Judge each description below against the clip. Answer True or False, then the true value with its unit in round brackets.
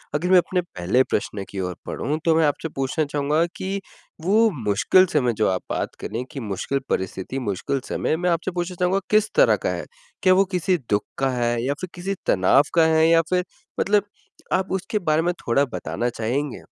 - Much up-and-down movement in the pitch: True (6.9 semitones)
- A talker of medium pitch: True (155 Hz)